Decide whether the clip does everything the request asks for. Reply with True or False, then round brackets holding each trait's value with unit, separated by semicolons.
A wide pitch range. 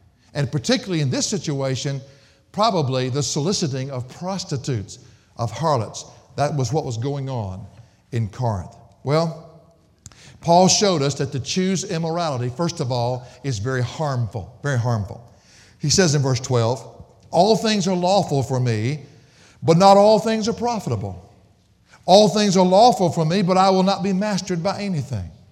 True (7.2 semitones)